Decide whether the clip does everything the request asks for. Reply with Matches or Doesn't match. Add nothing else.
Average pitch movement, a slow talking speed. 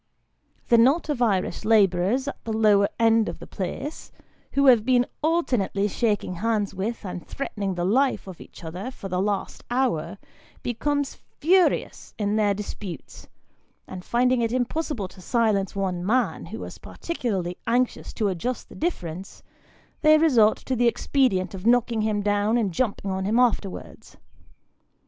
Doesn't match